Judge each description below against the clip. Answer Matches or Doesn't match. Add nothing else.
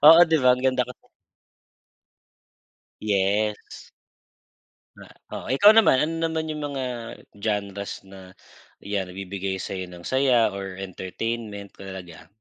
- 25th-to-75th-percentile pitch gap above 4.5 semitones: Matches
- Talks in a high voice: Doesn't match